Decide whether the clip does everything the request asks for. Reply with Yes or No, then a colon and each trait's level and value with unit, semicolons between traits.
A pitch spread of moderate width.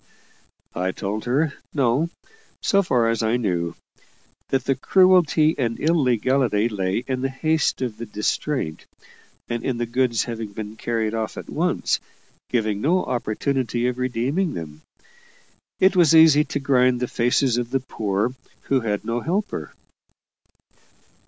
Yes: average, 3.9 semitones